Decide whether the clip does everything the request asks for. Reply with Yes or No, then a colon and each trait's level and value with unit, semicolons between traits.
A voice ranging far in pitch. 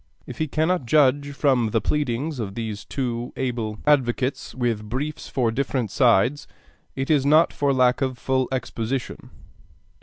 No: average, 3.3 semitones